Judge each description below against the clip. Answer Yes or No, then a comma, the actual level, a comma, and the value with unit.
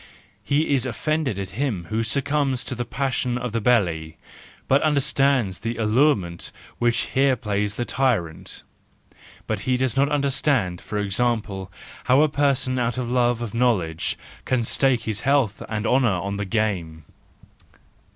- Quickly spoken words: No, average, 155 wpm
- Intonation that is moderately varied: Yes, average, 4.7 semitones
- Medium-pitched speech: No, low, 120 Hz